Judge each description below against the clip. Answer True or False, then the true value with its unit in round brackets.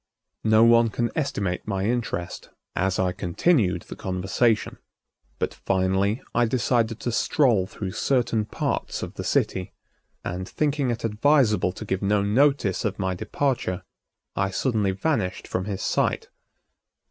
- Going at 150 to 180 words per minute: False (140 wpm)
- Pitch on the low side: True (105 Hz)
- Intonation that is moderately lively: True (4.2 semitones)